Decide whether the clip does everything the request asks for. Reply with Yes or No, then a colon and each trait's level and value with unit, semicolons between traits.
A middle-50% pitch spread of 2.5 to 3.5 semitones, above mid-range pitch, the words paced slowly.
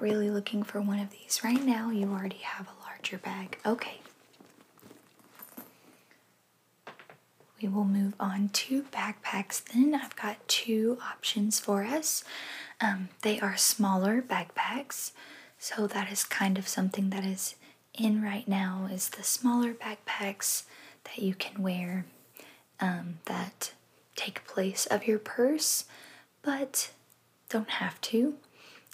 Yes: average, 3.1 semitones; high, 210 Hz; slow, 130 wpm